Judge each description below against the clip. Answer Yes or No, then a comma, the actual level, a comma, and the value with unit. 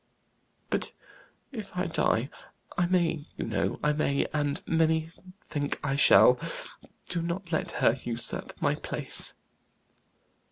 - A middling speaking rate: No, slow, 125 wpm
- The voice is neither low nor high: Yes, medium, 160 Hz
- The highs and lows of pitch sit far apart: No, average, 3.1 semitones